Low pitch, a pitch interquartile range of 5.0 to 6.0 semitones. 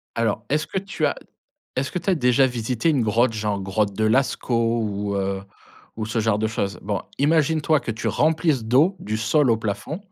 Yes: low, 115 Hz; wide, 5.4 semitones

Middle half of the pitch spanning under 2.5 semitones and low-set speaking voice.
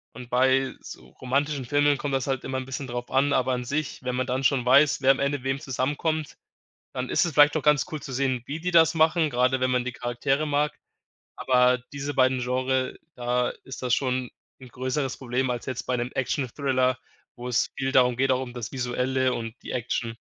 Yes: narrow, 1.9 semitones; low, 130 Hz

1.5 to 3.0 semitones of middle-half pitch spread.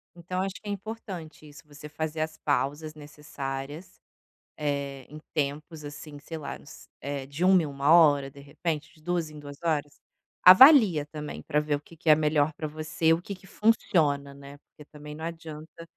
Yes: narrow, 2.4 semitones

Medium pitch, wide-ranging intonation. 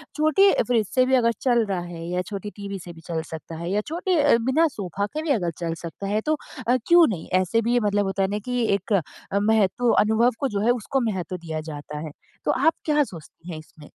No: high, 205 Hz; wide, 6.1 semitones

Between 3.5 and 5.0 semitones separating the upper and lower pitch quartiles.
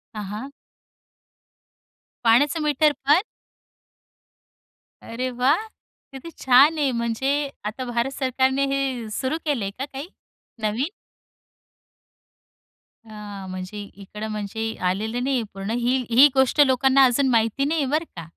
Yes: average, 3.8 semitones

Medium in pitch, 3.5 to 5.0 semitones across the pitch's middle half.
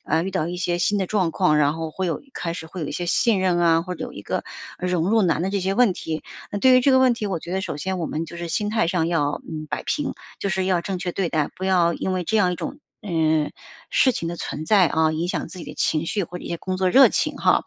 No: medium, 180 Hz; average, 2.7 semitones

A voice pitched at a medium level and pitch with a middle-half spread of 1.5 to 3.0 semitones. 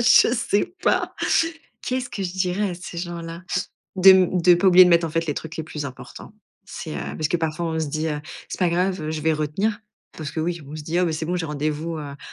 Yes: medium, 170 Hz; average, 2.7 semitones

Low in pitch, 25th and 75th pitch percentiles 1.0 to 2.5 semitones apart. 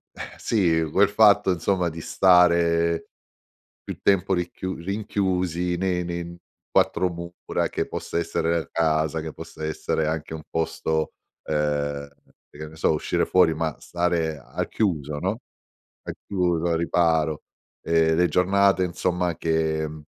Yes: very low, 85 Hz; narrow, 2.2 semitones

